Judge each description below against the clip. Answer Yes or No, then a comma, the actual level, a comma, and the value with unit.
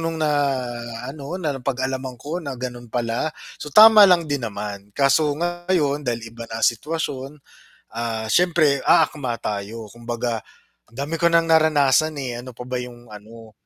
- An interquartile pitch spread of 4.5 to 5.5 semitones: Yes, average, 5.0 semitones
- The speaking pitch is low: Yes, low, 130 Hz